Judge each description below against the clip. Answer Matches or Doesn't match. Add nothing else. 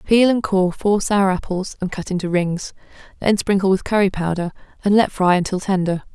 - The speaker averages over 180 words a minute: Matches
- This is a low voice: Doesn't match